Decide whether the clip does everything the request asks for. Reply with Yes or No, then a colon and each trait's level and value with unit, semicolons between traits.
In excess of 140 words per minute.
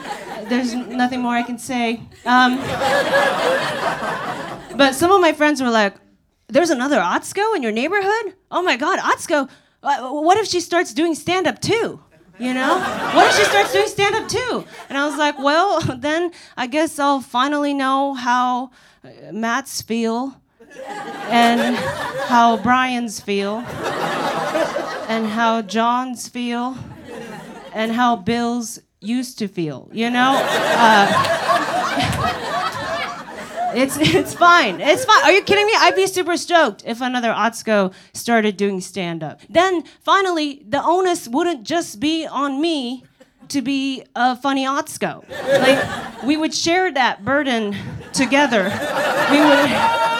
No: slow, 135 wpm